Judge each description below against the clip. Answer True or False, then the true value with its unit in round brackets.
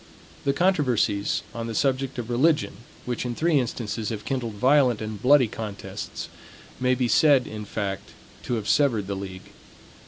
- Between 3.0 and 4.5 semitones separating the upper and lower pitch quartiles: True (4.2 semitones)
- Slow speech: False (160 wpm)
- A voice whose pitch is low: True (120 Hz)